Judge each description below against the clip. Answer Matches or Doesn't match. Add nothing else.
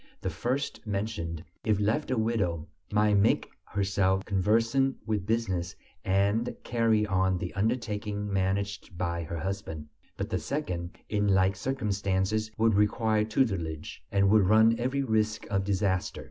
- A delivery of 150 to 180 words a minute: Doesn't match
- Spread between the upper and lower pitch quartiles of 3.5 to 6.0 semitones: Doesn't match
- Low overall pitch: Matches